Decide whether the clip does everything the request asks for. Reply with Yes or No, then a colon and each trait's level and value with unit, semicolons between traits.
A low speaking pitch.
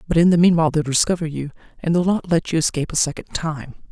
No: medium, 160 Hz